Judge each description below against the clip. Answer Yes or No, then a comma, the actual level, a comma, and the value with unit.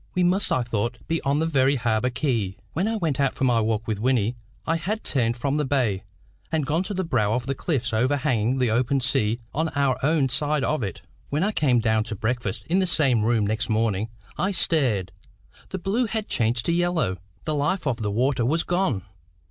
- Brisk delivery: Yes, fast, 215 wpm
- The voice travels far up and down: Yes, wide, 5.7 semitones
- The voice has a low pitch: Yes, low, 130 Hz